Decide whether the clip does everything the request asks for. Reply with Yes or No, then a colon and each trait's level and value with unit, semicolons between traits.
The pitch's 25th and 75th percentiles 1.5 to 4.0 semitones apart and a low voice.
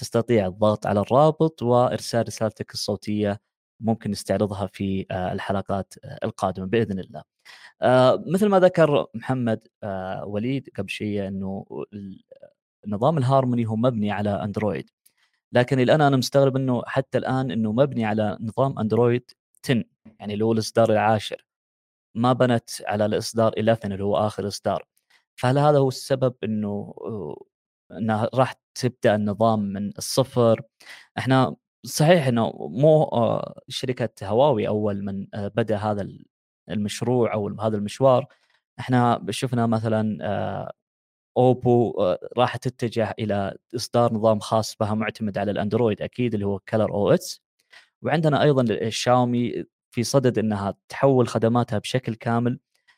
Yes: average, 3.5 semitones; low, 115 Hz